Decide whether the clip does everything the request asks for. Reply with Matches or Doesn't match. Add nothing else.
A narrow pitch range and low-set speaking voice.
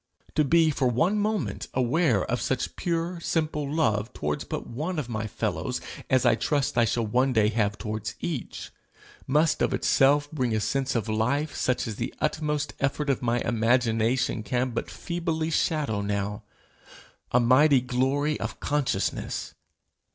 Doesn't match